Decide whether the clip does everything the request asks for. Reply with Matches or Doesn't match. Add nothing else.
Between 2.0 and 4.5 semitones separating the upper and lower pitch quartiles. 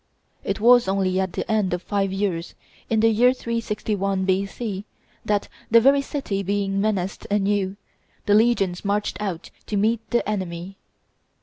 Matches